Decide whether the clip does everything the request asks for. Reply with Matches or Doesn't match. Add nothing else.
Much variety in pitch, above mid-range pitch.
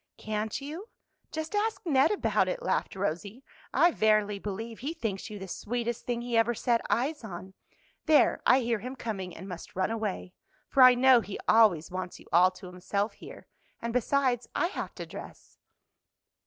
Doesn't match